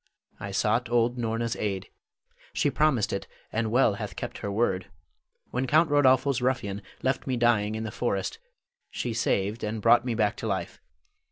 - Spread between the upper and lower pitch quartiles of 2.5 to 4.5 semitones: Yes, average, 3.2 semitones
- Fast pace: No, average, 170 wpm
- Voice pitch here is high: No, low, 115 Hz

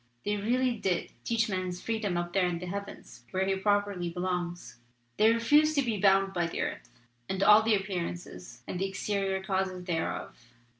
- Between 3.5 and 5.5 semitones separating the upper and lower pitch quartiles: No, average, 2.7 semitones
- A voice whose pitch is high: Yes, high, 195 Hz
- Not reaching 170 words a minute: No, average, 180 wpm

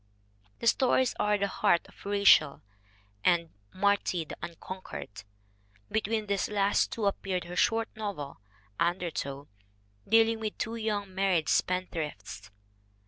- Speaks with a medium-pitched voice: No, high, 195 Hz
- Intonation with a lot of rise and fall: No, average, 3.8 semitones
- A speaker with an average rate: No, slow, 130 wpm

